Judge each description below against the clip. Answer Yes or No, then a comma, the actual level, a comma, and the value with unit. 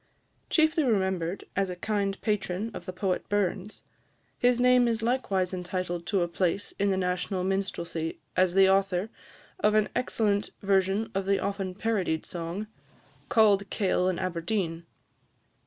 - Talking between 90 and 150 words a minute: Yes, average, 145 wpm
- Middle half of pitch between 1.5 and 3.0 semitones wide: Yes, narrow, 2.5 semitones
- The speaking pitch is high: Yes, high, 195 Hz